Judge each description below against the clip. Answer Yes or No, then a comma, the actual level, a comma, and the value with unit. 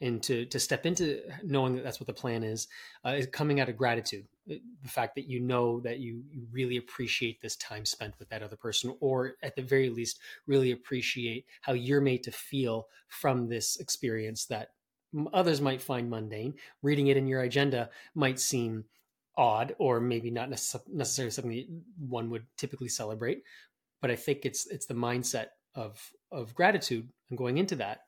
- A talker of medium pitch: No, low, 125 Hz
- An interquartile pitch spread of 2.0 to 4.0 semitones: Yes, narrow, 2.6 semitones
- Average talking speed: Yes, average, 185 wpm